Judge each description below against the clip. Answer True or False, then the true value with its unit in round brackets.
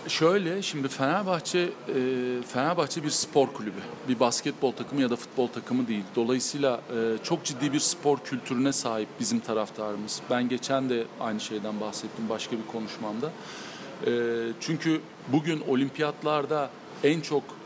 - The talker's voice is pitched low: True (130 Hz)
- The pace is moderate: True (130 wpm)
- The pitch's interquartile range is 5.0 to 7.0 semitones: False (4.3 semitones)